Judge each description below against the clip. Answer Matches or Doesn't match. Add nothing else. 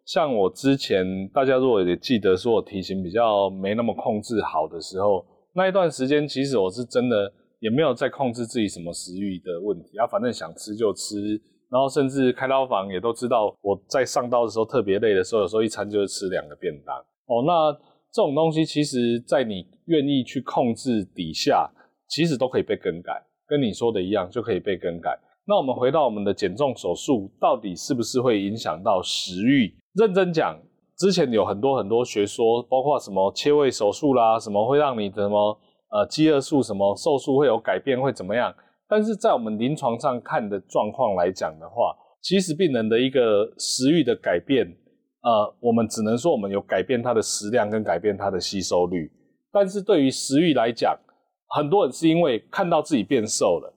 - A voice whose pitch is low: Matches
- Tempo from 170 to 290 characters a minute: Doesn't match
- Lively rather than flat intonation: Matches